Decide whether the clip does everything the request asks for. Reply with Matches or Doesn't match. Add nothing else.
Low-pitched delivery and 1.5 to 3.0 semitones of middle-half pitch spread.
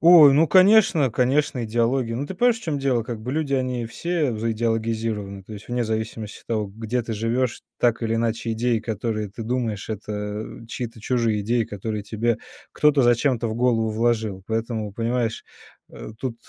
Matches